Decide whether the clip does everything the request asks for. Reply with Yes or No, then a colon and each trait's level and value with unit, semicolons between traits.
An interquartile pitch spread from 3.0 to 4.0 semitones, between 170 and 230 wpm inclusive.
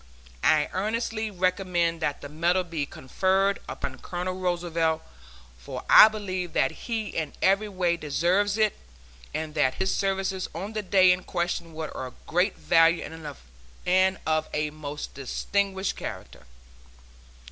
No: average, 3.3 semitones; slow, 135 wpm